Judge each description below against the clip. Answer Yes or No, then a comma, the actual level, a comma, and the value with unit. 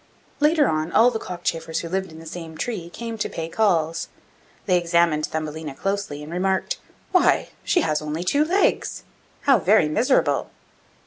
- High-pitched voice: No, medium, 175 Hz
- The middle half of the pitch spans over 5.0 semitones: Yes, wide, 5.6 semitones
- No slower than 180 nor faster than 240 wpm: No, average, 170 wpm